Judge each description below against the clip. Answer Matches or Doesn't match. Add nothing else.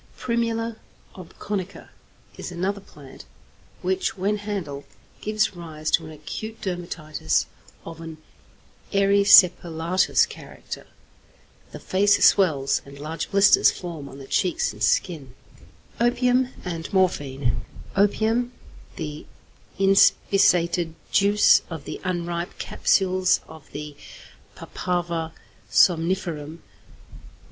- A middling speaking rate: Doesn't match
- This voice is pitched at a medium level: Matches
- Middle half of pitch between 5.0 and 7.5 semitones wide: Doesn't match